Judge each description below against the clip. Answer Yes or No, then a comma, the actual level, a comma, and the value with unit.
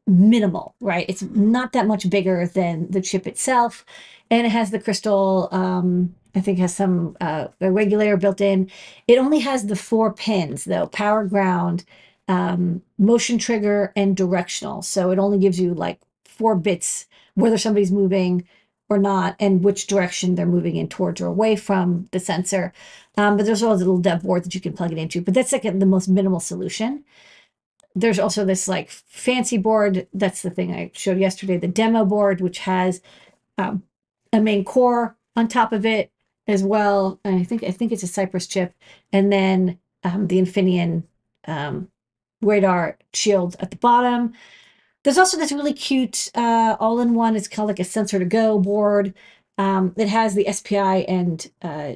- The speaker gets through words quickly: No, average, 180 wpm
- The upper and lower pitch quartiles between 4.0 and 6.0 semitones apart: No, average, 2.9 semitones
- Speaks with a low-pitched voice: No, high, 195 Hz